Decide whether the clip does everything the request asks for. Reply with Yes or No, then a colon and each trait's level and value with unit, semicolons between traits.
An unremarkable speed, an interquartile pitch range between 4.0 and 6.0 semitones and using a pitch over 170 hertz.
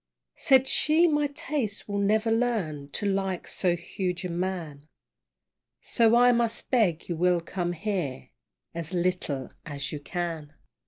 Yes: average, 145 wpm; average, 5.3 semitones; medium, 185 Hz